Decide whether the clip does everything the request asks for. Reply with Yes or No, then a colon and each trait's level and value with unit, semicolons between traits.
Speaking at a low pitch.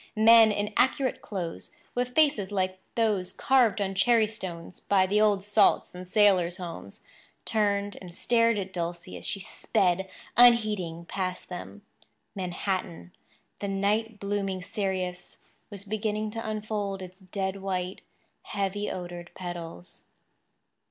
No: high, 195 Hz